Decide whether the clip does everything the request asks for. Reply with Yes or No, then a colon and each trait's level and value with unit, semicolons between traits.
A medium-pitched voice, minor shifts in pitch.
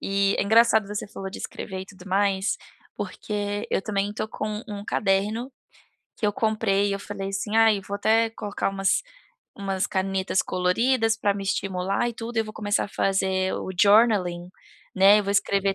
No: high, 200 Hz; narrow, 1.8 semitones